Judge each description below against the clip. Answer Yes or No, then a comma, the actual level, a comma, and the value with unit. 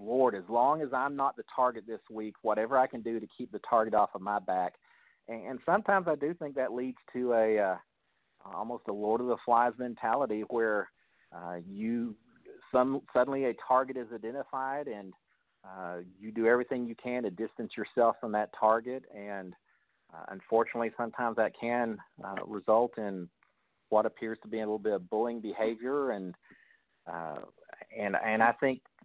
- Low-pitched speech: Yes, low, 115 Hz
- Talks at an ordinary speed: Yes, average, 180 wpm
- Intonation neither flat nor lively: Yes, average, 3.1 semitones